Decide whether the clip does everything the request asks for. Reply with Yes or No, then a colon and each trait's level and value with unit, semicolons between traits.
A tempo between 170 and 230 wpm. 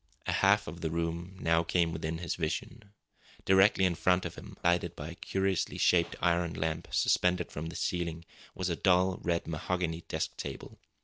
Yes: average, 175 wpm